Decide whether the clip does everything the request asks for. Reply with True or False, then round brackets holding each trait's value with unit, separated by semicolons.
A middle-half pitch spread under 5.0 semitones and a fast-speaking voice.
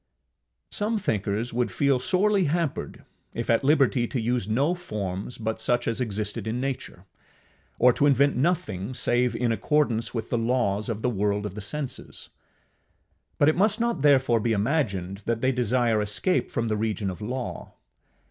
False (4.5 semitones; 165 wpm)